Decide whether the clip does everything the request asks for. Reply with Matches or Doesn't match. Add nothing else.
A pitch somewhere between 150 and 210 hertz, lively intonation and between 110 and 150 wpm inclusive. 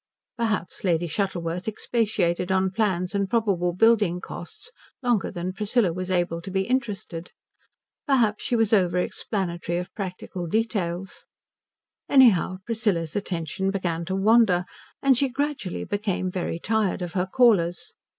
Doesn't match